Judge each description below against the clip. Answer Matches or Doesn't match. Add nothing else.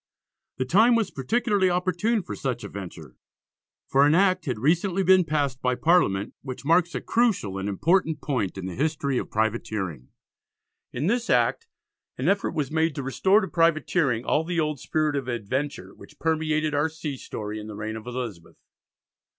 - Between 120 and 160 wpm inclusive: Doesn't match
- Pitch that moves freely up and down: Matches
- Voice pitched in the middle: Matches